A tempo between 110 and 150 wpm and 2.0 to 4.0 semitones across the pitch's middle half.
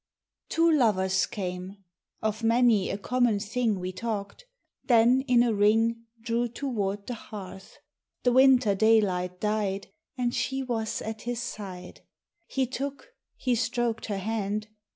Yes: slow, 135 wpm; average, 3.3 semitones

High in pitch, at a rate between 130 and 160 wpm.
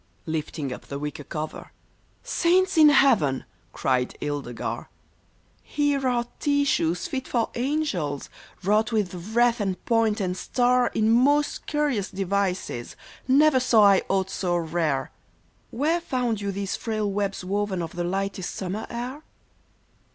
Yes: high, 205 Hz; average, 155 wpm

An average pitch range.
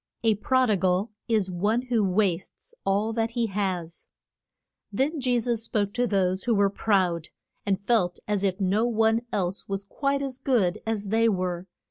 Yes: average, 3.4 semitones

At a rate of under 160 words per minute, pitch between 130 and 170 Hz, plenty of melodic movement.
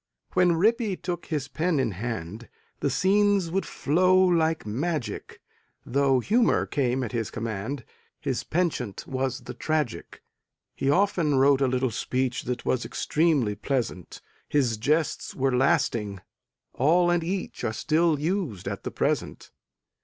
Yes: average, 140 wpm; medium, 140 Hz; wide, 5.9 semitones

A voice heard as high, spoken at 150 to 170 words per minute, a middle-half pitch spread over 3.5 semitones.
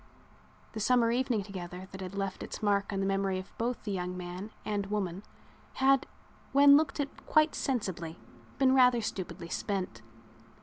Yes: high, 200 Hz; average, 165 wpm; average, 4.9 semitones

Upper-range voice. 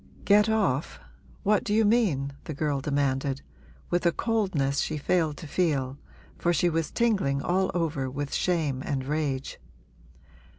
No: medium, 155 Hz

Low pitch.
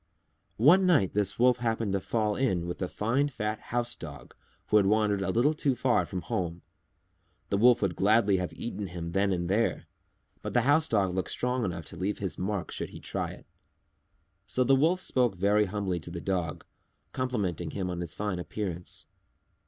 Yes: low, 105 Hz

